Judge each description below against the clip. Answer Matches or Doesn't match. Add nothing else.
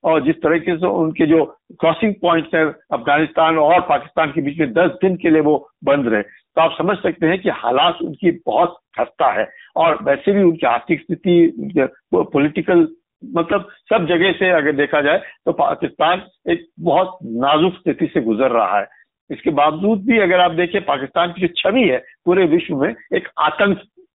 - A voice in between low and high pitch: Matches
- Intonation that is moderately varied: Matches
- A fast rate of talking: Doesn't match